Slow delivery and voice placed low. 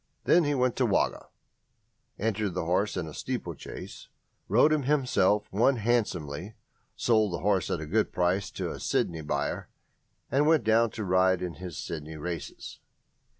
No: average, 165 wpm; low, 100 Hz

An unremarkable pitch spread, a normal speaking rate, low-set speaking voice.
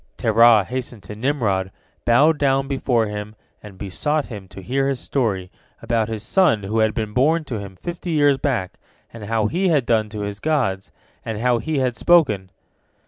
Yes: average, 4.8 semitones; average, 185 wpm; low, 115 Hz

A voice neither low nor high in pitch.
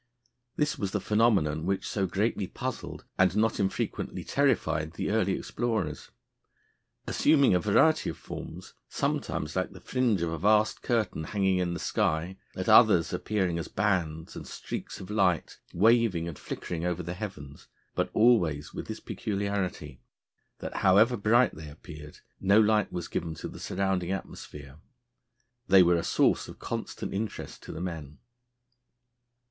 No: very low, 95 Hz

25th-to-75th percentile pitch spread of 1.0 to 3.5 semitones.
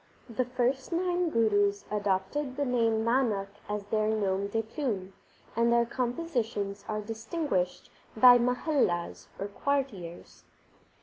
No: average, 4.1 semitones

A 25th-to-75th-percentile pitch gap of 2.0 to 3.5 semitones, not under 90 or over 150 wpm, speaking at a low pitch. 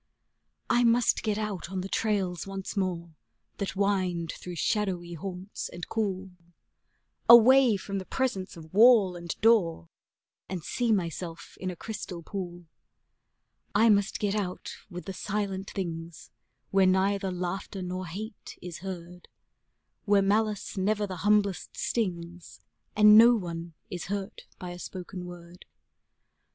No: average, 2.8 semitones; average, 140 wpm; high, 190 Hz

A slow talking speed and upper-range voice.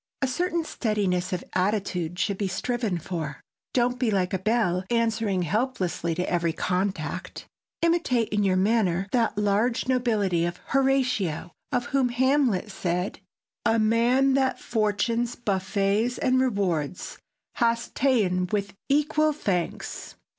Yes: slow, 130 wpm; high, 210 Hz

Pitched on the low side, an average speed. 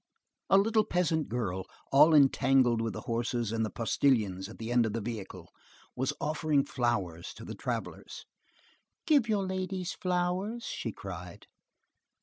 Yes: low, 130 Hz; average, 145 wpm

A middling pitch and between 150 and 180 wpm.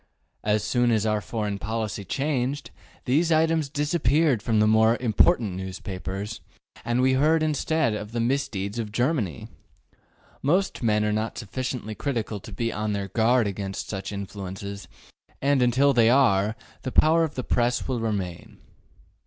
No: low, 115 Hz; average, 155 wpm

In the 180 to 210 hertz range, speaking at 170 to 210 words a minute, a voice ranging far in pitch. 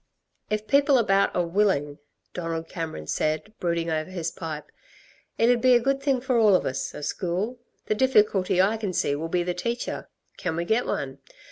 Yes: medium, 185 Hz; average, 190 wpm; wide, 5.8 semitones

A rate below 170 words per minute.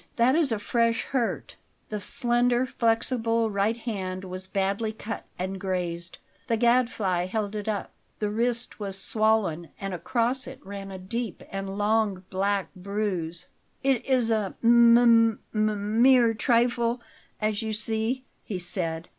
Yes: average, 145 wpm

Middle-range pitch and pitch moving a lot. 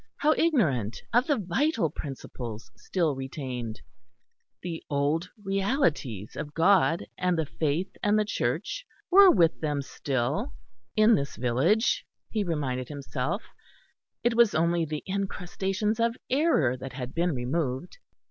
Yes: medium, 165 Hz; wide, 7.5 semitones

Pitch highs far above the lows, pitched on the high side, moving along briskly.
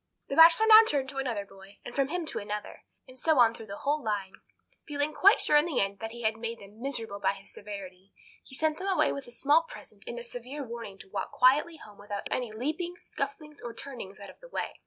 Yes: wide, 6.4 semitones; high, 245 Hz; fast, 240 wpm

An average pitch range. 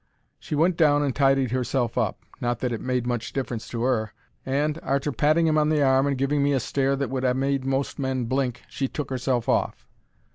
No: narrow, 2.1 semitones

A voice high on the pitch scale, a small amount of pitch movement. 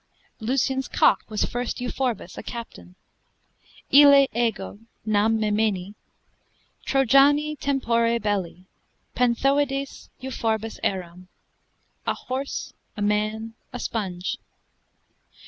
No: high, 230 Hz; average, 4.3 semitones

